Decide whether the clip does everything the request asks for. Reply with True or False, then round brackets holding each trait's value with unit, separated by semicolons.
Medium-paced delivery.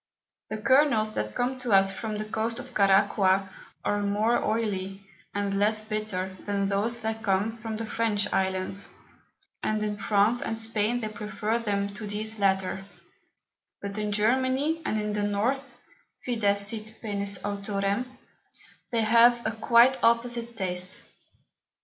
True (145 wpm)